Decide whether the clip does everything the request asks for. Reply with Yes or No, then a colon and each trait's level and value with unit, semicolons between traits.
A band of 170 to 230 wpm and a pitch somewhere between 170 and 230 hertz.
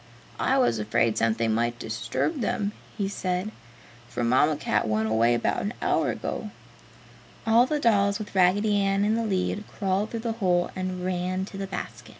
Yes: average, 175 wpm; medium, 185 Hz